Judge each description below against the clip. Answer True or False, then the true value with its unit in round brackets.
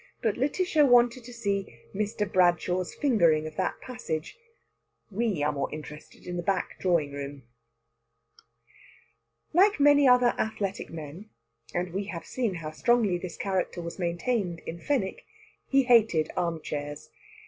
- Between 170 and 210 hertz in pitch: True (190 Hz)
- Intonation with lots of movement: True (6.3 semitones)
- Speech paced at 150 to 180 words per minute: False (135 wpm)